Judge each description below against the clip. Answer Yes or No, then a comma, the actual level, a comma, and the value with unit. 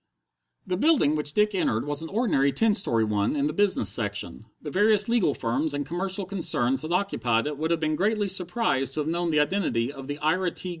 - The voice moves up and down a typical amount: No, wide, 5.9 semitones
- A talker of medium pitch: Yes, medium, 155 Hz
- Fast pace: Yes, fast, 215 wpm